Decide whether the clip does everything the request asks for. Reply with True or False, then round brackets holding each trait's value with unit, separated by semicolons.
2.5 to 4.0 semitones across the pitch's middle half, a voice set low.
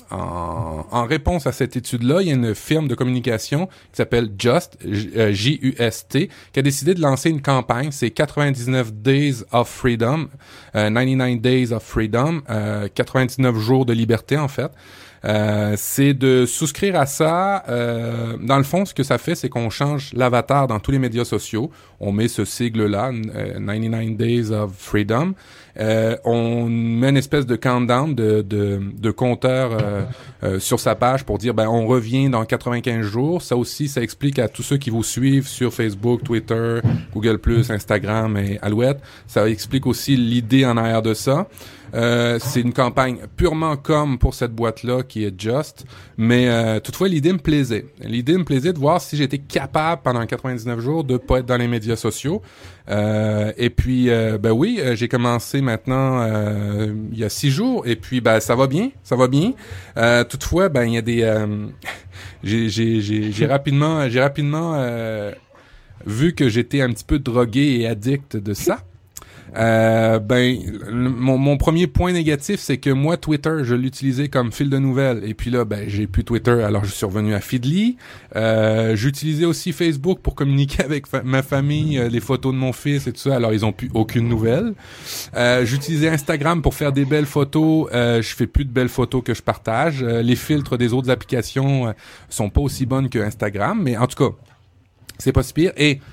True (3.6 semitones; 125 Hz)